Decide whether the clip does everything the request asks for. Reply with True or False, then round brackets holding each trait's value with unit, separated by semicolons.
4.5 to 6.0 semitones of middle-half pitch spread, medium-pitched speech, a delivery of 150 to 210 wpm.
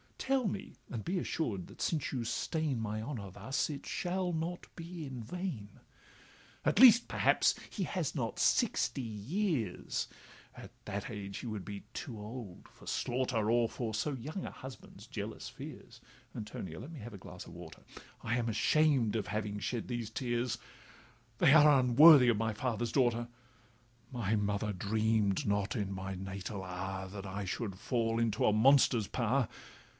False (5.0 semitones; 115 Hz; 165 wpm)